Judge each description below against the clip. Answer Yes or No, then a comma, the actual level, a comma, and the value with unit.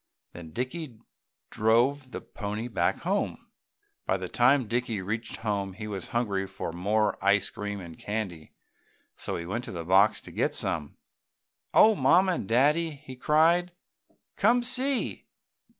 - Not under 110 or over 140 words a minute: No, average, 150 wpm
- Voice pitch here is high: No, low, 110 Hz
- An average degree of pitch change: No, wide, 6.6 semitones